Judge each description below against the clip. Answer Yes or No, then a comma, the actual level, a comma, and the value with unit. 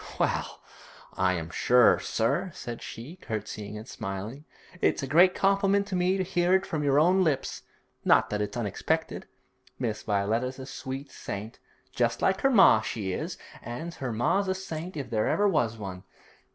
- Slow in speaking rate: No, average, 175 wpm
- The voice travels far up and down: Yes, wide, 8.9 semitones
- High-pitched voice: No, low, 130 Hz